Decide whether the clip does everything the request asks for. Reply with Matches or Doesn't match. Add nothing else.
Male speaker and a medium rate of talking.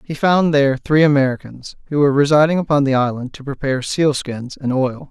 Matches